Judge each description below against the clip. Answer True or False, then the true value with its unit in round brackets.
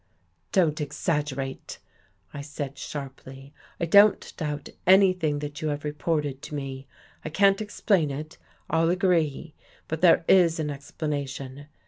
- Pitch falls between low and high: True (150 Hz)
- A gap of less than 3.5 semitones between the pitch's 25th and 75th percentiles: True (3.0 semitones)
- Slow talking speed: False (145 wpm)